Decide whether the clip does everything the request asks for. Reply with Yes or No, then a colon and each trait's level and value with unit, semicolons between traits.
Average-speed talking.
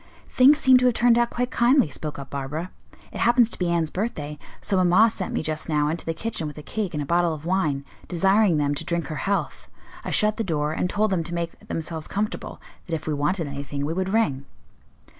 No: fast, 235 wpm